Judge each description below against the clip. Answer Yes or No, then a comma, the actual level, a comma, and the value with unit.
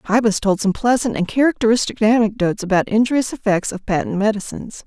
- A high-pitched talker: Yes, high, 215 Hz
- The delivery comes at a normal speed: Yes, average, 160 wpm